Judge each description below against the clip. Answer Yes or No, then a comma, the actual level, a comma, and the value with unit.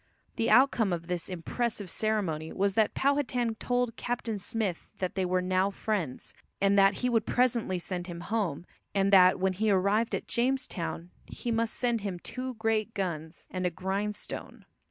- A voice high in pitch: Yes, high, 200 Hz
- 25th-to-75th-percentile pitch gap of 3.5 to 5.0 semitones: Yes, average, 3.8 semitones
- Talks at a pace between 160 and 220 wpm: Yes, average, 170 wpm